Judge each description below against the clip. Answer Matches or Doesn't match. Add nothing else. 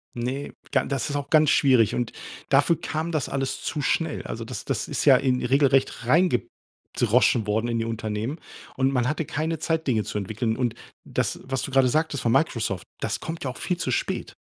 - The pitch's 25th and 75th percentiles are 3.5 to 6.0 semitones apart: Matches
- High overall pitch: Doesn't match